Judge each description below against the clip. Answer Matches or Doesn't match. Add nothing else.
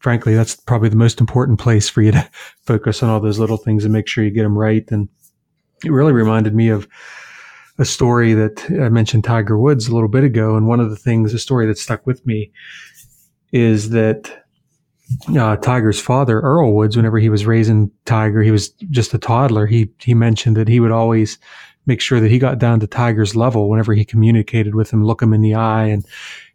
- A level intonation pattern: Matches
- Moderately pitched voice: Doesn't match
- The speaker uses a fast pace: Matches